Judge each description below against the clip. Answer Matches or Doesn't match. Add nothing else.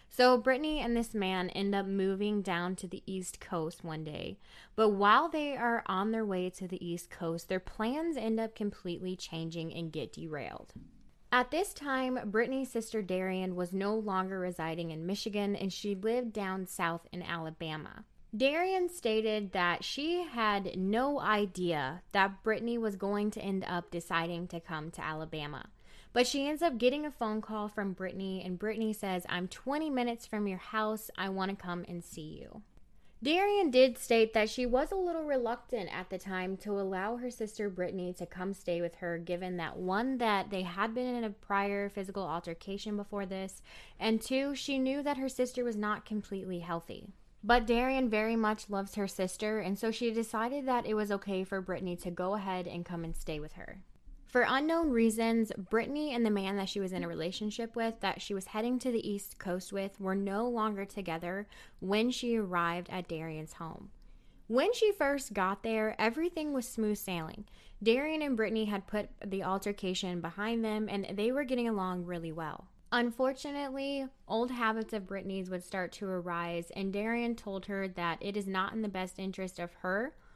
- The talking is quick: Doesn't match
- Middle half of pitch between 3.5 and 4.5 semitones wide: Matches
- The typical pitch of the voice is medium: Doesn't match